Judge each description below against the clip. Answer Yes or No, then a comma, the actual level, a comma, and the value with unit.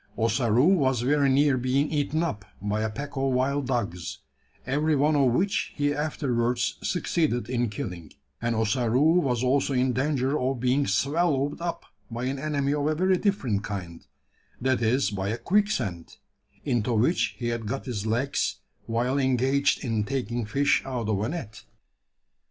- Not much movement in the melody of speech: No, average, 3.6 semitones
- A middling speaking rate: Yes, average, 165 wpm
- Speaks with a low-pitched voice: Yes, low, 130 Hz